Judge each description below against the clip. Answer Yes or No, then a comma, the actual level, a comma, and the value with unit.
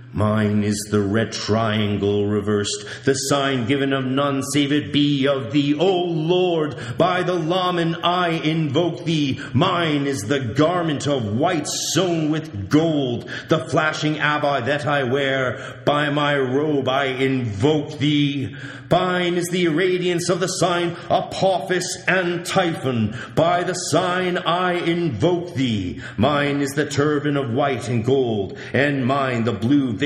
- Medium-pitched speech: Yes, medium, 145 Hz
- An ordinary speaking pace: Yes, average, 150 wpm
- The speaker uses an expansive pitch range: No, average, 4.3 semitones